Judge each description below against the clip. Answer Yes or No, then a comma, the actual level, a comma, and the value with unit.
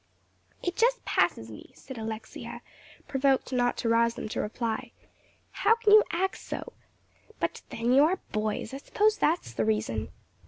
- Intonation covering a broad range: Yes, wide, 8.1 semitones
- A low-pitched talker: No, high, 245 Hz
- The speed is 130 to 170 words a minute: Yes, average, 160 wpm